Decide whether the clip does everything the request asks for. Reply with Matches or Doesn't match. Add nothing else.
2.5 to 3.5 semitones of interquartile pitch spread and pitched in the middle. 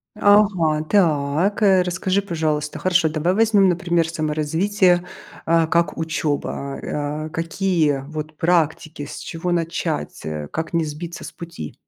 Matches